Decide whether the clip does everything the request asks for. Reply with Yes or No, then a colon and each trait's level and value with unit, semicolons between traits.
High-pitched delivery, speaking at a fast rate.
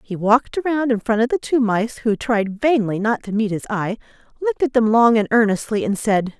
Yes: high, 230 Hz; fast, 235 wpm